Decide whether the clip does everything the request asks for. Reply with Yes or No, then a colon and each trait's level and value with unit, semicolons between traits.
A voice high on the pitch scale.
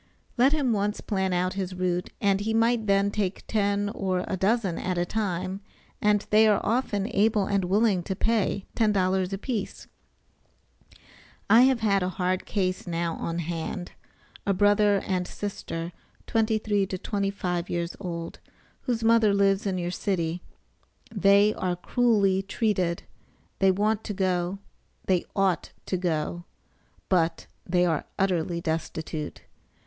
Yes: high, 195 Hz